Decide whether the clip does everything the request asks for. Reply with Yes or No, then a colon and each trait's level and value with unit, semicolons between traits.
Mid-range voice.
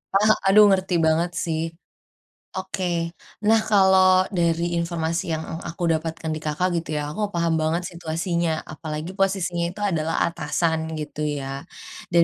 Yes: medium, 170 Hz